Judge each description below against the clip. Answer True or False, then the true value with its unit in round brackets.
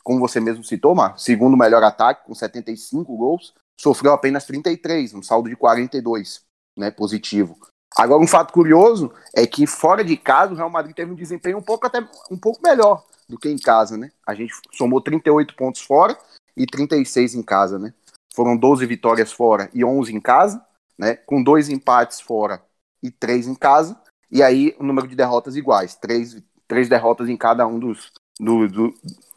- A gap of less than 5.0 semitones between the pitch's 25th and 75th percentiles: False (5.3 semitones)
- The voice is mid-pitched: False (130 Hz)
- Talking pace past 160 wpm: True (185 wpm)